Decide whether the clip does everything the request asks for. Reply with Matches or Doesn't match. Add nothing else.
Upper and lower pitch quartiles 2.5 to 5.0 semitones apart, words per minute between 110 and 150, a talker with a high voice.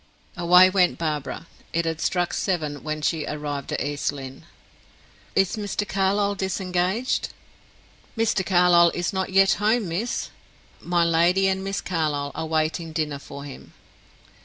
Doesn't match